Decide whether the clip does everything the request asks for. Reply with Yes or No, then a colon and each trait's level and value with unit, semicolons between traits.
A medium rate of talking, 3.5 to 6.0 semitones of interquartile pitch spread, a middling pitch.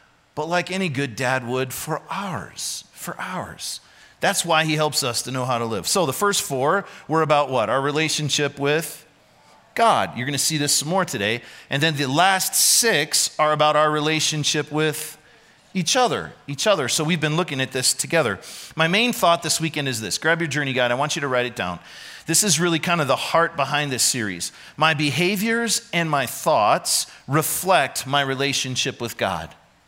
Yes: average, 195 wpm; average, 3.9 semitones; medium, 150 Hz